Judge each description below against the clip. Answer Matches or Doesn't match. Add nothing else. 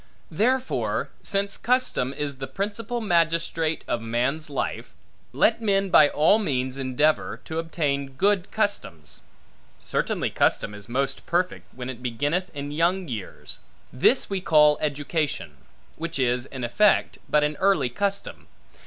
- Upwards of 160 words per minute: Doesn't match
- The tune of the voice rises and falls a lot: Matches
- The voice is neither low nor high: Matches